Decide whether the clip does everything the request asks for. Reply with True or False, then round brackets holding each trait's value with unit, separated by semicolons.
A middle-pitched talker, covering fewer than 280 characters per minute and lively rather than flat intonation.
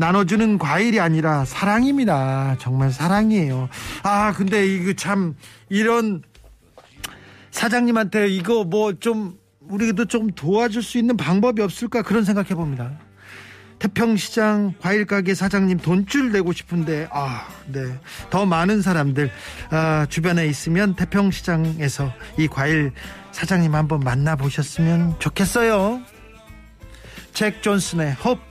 True (180 Hz; 265 characters per minute; 6.7 semitones)